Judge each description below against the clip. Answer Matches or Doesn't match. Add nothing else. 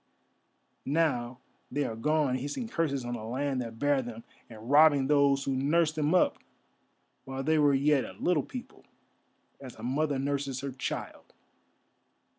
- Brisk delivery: Doesn't match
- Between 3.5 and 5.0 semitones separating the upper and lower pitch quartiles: Doesn't match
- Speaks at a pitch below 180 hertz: Matches